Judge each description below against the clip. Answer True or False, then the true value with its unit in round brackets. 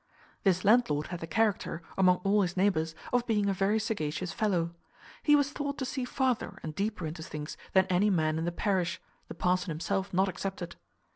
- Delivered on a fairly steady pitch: False (3.8 semitones)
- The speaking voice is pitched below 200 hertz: True (190 Hz)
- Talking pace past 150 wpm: True (195 wpm)